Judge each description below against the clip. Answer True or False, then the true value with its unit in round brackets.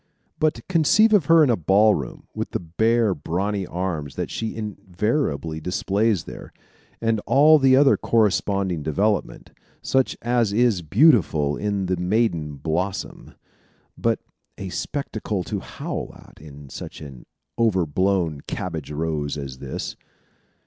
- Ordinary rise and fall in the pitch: False (6.3 semitones)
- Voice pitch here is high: False (95 Hz)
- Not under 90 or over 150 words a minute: True (135 wpm)